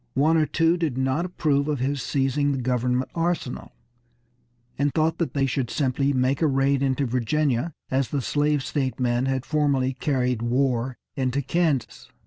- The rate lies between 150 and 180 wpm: Yes, average, 160 wpm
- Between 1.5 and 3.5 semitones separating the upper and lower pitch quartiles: Yes, narrow, 2.6 semitones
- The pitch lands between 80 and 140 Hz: Yes, low, 135 Hz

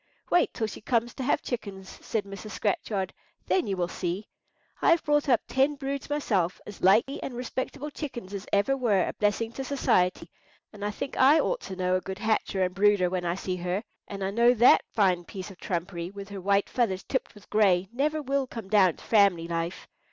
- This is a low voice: No, high, 205 Hz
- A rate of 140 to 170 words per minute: No, fast, 205 wpm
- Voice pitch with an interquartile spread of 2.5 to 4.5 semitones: No, average, 5.1 semitones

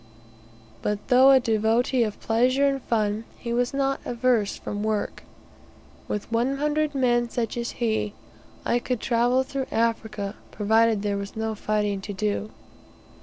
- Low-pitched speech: No, high, 230 Hz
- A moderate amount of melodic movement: Yes, average, 3.1 semitones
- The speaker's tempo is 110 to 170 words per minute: Yes, average, 150 wpm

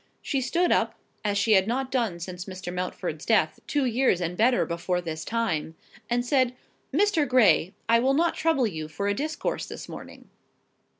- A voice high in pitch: Yes, high, 230 Hz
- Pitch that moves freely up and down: Yes, wide, 6.5 semitones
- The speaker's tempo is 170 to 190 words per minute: Yes, average, 180 wpm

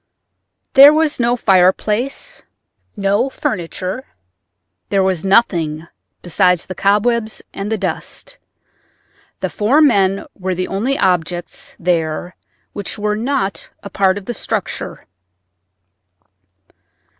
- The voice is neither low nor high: No, high, 195 Hz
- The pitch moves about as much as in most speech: Yes, average, 4.2 semitones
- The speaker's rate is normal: No, slow, 110 wpm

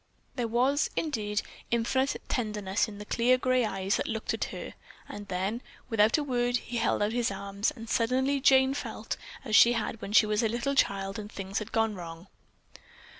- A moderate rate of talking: Yes, average, 190 wpm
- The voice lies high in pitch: Yes, high, 225 Hz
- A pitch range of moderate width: Yes, average, 3.1 semitones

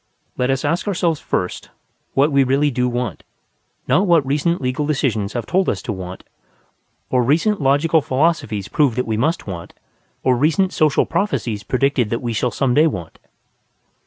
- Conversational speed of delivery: Yes, average, 170 wpm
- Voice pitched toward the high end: No, low, 135 Hz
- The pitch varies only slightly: No, average, 4.7 semitones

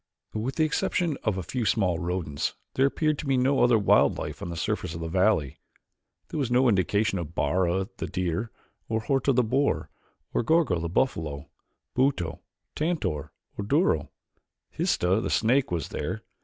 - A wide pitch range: Yes, wide, 7.4 semitones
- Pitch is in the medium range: No, low, 110 Hz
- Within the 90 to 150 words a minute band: No, average, 175 wpm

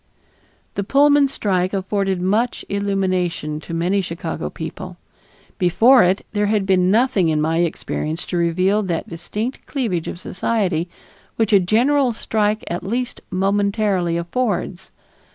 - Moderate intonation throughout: Yes, average, 3.6 semitones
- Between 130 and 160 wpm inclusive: Yes, slow, 135 wpm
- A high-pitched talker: Yes, high, 195 Hz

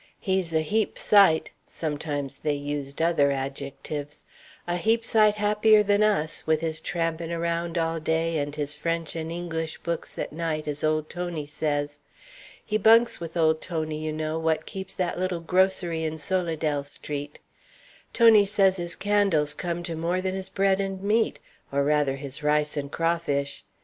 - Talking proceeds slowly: No, average, 165 wpm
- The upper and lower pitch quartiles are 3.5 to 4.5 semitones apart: Yes, average, 3.8 semitones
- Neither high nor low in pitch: Yes, medium, 165 Hz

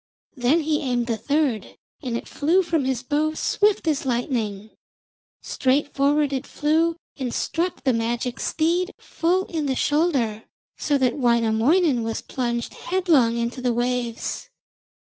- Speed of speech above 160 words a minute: No, average, 145 wpm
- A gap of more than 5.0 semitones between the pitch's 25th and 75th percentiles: No, average, 4.7 semitones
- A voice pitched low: No, very high, 265 Hz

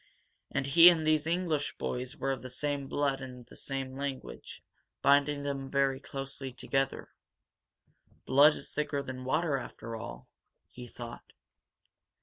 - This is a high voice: No, low, 135 Hz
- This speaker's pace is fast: No, average, 140 wpm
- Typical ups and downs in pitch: No, narrow, 1.7 semitones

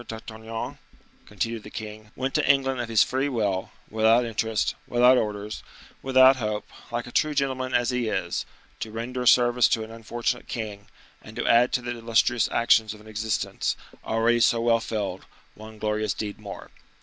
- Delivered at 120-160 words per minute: No, average, 175 wpm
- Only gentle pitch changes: Yes, narrow, 2.3 semitones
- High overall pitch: No, low, 115 Hz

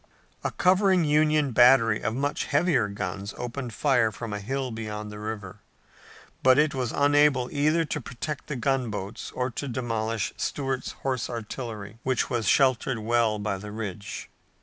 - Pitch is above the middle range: No, low, 125 Hz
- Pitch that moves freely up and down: No, average, 4.3 semitones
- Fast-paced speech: No, average, 155 wpm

